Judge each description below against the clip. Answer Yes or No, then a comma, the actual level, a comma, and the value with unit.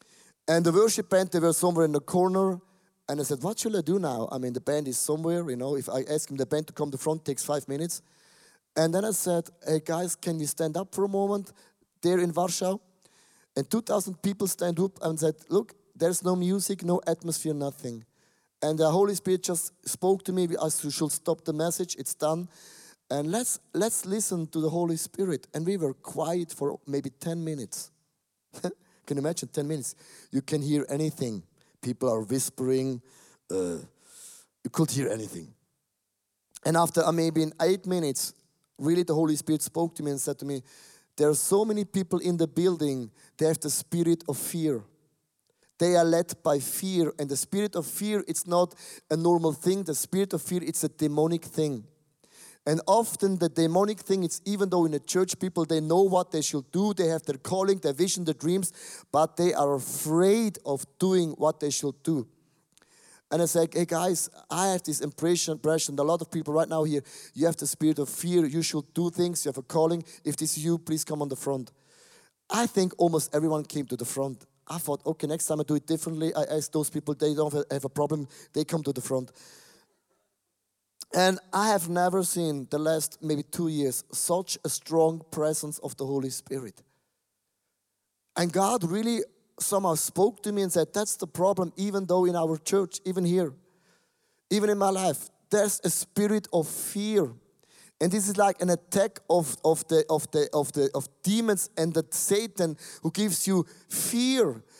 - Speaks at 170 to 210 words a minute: Yes, average, 200 wpm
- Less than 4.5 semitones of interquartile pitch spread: Yes, average, 3.7 semitones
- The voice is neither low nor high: Yes, medium, 165 Hz